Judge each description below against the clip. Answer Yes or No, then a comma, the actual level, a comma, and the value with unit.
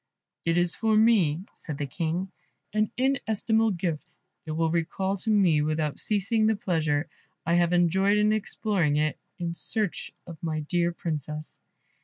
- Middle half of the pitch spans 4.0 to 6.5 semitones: Yes, average, 4.8 semitones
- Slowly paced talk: No, average, 155 wpm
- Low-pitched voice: No, medium, 175 Hz